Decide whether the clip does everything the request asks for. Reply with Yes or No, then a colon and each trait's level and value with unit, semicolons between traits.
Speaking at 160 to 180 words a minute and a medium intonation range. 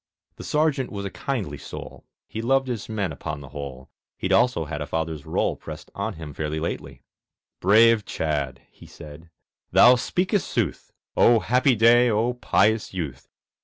No: average, 165 wpm; wide, 7.8 semitones